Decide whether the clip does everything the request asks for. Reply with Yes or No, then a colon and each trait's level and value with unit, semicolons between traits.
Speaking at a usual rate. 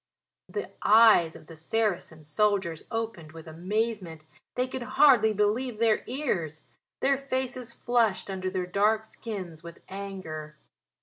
No: slow, 130 wpm